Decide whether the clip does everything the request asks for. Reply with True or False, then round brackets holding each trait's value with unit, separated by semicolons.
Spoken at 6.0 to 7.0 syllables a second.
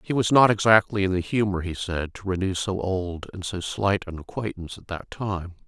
False (5.1 syllables/s)